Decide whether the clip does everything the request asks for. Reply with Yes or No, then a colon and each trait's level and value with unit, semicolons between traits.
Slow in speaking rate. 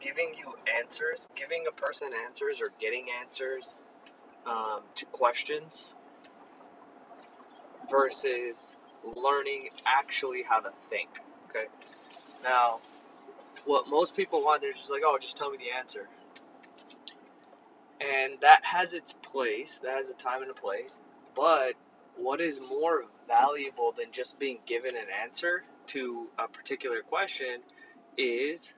Yes: slow, 125 wpm